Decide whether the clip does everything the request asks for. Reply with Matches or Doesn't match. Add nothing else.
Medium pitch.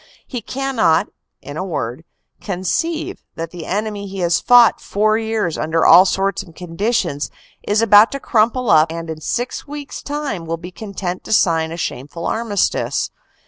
Doesn't match